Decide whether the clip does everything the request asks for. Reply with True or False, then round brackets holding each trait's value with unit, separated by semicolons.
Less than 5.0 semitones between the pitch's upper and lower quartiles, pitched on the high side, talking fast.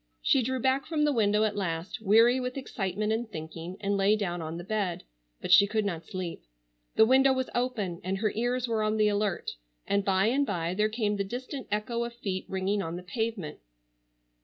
True (4.0 semitones; 210 Hz; 210 wpm)